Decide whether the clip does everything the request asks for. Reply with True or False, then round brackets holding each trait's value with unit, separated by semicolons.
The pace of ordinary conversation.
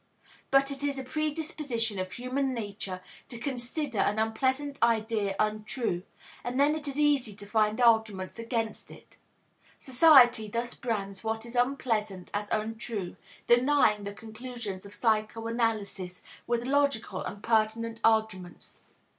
False (130 wpm)